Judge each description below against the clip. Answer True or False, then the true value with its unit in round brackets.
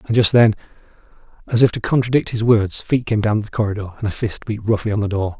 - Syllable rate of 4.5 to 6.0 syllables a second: False (6.2 syllables/s)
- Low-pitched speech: True (110 Hz)